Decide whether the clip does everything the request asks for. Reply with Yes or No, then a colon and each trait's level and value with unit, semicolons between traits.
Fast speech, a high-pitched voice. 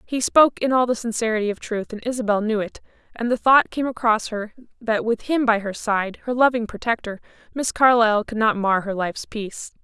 Yes: fast, 215 wpm; high, 225 Hz